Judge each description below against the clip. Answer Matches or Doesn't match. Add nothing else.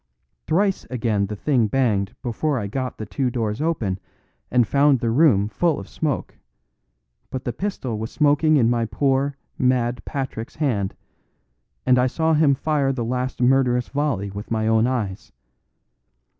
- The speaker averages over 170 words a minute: Doesn't match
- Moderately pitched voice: Doesn't match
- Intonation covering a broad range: Doesn't match